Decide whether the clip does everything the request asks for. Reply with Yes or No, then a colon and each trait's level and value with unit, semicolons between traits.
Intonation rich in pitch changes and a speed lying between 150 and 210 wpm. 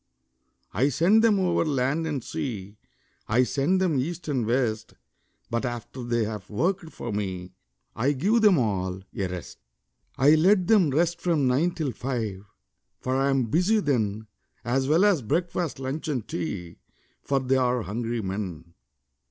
Yes: wide, 7.0 semitones; average, 160 wpm